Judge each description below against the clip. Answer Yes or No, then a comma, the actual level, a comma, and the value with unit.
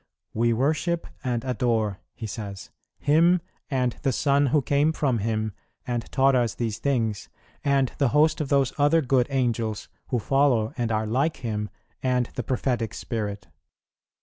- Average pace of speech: Yes, average, 155 wpm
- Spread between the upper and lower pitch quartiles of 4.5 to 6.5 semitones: No, average, 3.8 semitones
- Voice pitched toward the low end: Yes, low, 125 Hz